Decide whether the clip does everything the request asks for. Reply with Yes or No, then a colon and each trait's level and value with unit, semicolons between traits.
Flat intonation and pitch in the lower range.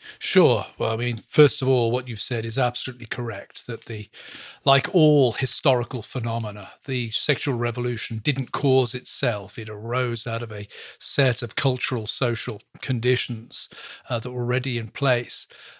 Yes: narrow, 2.2 semitones; low, 120 Hz